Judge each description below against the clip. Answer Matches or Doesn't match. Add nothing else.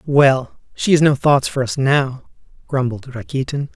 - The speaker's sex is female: Doesn't match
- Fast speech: Doesn't match